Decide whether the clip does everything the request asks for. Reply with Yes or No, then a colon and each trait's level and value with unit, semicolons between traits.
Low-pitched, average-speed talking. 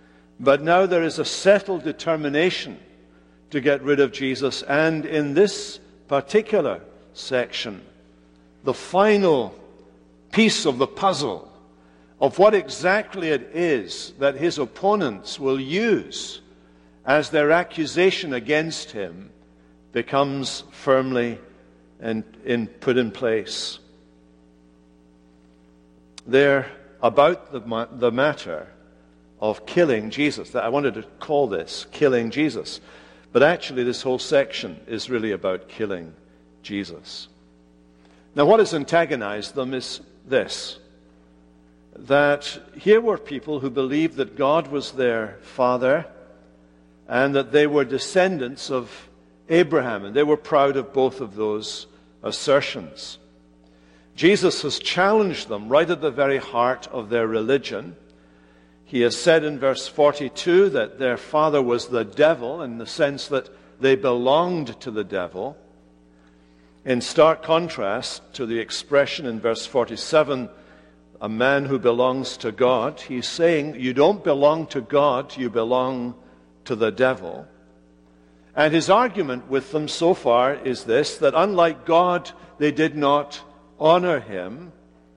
No: low, 130 Hz; slow, 130 wpm